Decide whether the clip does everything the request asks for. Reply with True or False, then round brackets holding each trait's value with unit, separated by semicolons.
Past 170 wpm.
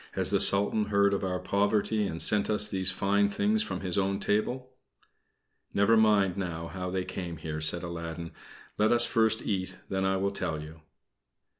True (180 wpm)